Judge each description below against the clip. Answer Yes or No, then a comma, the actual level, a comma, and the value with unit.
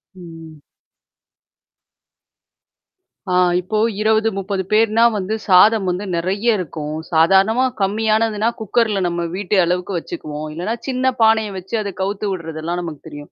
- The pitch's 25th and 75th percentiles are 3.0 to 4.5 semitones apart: Yes, average, 4.1 semitones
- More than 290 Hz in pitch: No, high, 195 Hz